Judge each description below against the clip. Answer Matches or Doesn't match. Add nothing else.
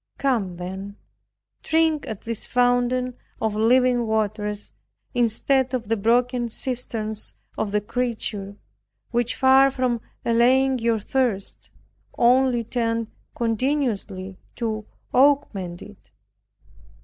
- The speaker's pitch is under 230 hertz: Doesn't match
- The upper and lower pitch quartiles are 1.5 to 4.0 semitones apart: Matches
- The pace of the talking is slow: Matches